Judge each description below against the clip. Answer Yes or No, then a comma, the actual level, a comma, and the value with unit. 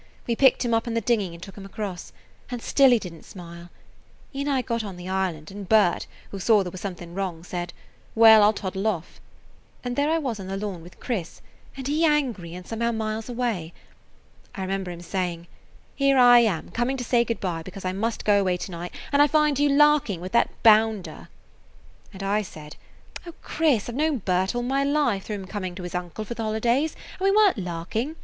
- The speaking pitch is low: No, high, 215 Hz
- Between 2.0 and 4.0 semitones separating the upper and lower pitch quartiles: No, average, 5.0 semitones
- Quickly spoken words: Yes, fast, 225 wpm